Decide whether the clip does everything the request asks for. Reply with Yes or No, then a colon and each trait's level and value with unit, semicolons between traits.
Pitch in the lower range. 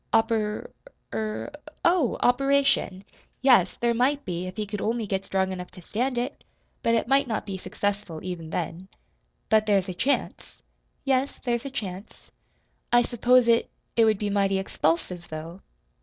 No: high, 215 Hz